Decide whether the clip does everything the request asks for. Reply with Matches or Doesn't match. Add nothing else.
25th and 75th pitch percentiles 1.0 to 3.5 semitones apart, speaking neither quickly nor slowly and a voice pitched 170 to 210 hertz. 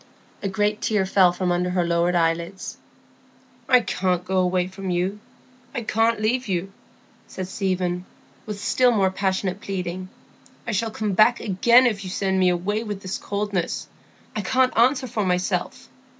Matches